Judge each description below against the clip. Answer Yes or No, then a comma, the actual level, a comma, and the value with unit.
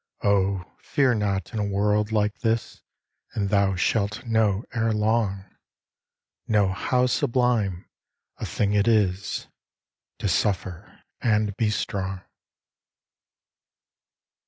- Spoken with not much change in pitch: Yes, narrow, 2.2 semitones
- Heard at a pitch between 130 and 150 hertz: No, low, 105 Hz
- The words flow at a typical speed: No, slow, 110 wpm